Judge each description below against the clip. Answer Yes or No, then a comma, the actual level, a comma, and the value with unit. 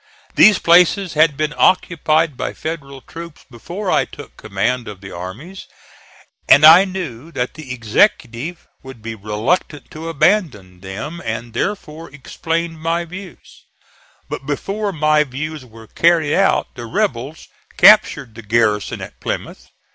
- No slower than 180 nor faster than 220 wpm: No, average, 140 wpm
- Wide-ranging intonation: Yes, wide, 6.5 semitones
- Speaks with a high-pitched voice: No, medium, 150 Hz